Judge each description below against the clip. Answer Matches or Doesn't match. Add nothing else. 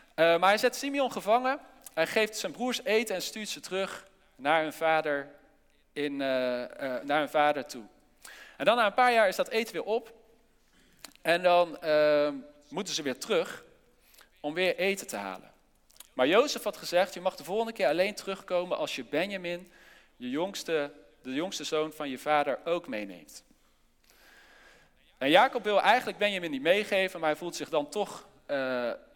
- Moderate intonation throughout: Doesn't match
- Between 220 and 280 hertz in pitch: Doesn't match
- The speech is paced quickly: Doesn't match